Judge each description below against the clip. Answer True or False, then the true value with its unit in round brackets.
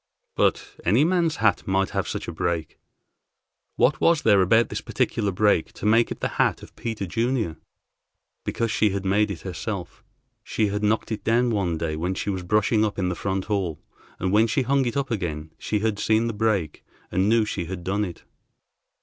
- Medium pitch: False (105 Hz)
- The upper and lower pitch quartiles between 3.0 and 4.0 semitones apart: True (3.4 semitones)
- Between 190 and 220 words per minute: True (200 wpm)